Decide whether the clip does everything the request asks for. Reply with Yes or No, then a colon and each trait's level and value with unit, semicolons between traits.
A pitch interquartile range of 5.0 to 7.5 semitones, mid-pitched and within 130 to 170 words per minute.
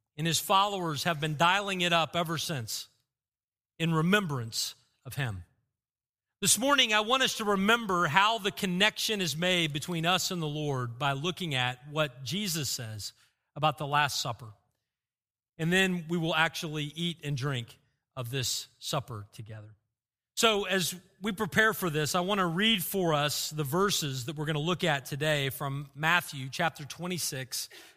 Yes: average, 5.3 semitones; medium, 155 Hz; average, 165 wpm